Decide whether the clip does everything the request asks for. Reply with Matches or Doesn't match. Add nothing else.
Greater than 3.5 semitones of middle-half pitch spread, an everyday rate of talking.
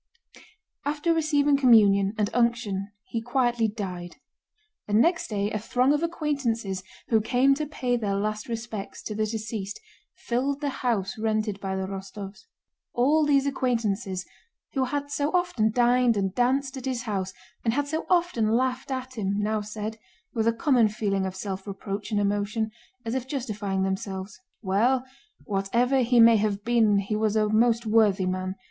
Matches